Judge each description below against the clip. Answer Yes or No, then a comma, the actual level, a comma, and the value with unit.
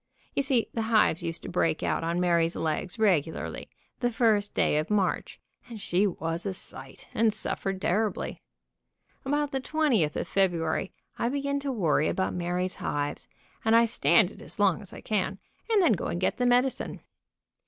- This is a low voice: No, high, 200 Hz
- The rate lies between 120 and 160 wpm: No, average, 180 wpm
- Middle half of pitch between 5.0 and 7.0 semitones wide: Yes, average, 5.3 semitones